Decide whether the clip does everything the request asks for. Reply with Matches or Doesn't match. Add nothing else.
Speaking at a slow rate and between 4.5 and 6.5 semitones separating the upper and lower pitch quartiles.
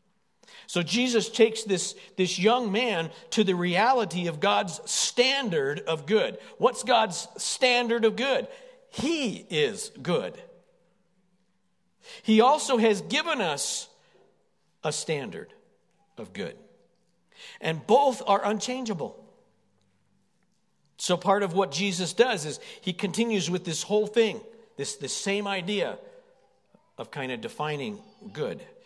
Matches